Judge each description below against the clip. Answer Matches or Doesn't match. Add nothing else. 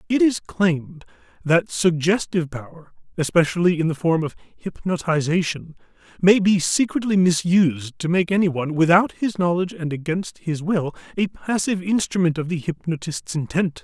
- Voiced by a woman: Doesn't match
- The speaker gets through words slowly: Doesn't match